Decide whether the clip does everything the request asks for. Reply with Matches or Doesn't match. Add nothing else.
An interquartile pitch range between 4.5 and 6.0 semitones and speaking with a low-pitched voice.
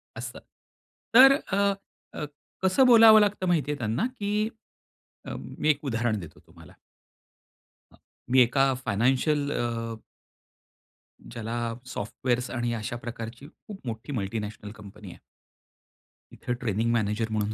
Matches